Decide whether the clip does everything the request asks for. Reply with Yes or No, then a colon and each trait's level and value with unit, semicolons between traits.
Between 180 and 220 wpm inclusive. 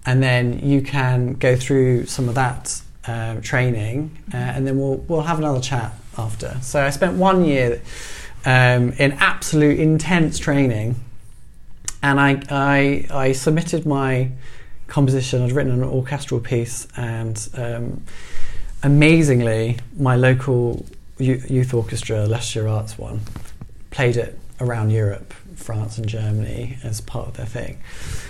No: slow, 135 wpm